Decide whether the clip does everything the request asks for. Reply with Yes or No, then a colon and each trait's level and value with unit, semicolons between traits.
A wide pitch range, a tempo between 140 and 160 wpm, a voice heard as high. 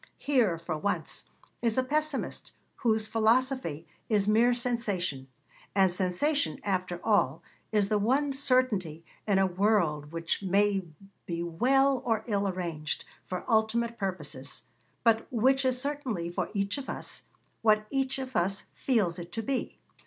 Yes: wide, 5.8 semitones; average, 145 wpm; high, 215 Hz